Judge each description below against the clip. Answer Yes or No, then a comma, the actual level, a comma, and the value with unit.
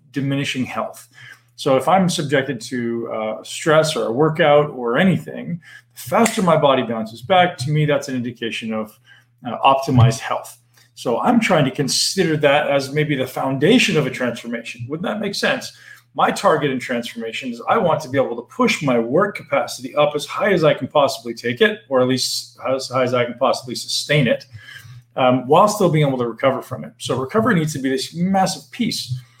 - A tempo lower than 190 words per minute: No, average, 200 wpm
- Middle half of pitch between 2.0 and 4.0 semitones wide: No, average, 4.4 semitones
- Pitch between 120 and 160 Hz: Yes, low, 135 Hz